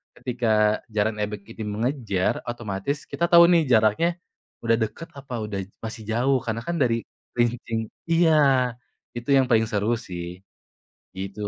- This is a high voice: No, low, 115 Hz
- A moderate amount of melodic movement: Yes, average, 3.6 semitones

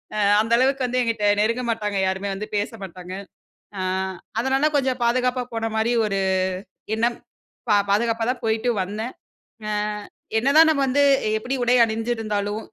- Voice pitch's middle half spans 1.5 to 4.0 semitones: Yes, average, 2.9 semitones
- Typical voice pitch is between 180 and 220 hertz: No, high, 230 Hz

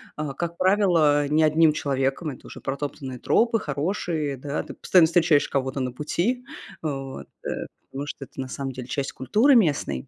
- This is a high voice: No, medium, 145 Hz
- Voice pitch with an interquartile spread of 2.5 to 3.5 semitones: No, average, 4.0 semitones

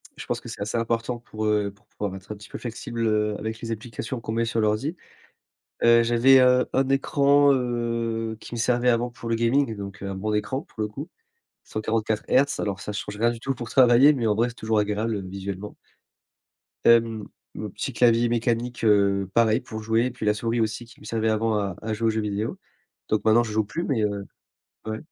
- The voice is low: Yes, low, 115 Hz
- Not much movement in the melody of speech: Yes, narrow, 2.1 semitones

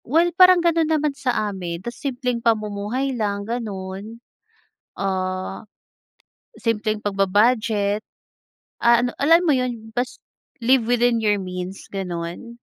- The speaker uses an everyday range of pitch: Yes, average, 4.1 semitones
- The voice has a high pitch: Yes, high, 225 Hz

